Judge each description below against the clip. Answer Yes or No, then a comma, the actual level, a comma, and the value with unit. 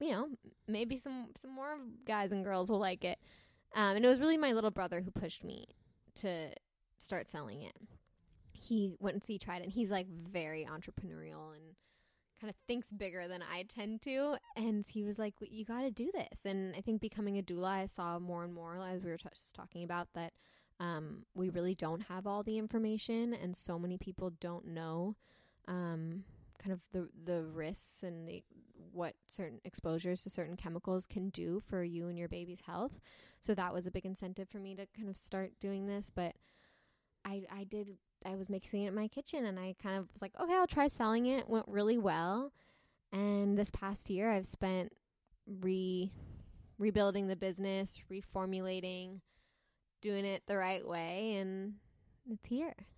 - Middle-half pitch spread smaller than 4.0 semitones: Yes, average, 3.0 semitones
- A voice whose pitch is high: Yes, high, 195 Hz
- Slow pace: No, average, 190 wpm